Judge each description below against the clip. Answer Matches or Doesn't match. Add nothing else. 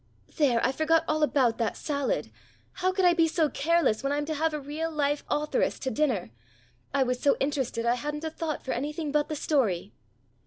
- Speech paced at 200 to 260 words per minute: Matches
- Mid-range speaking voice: Doesn't match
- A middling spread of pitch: Matches